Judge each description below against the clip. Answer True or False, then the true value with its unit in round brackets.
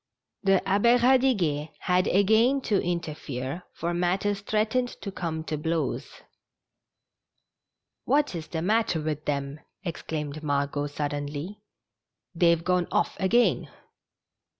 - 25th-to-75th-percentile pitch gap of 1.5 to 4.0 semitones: False (5.2 semitones)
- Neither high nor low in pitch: True (175 Hz)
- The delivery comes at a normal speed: False (120 wpm)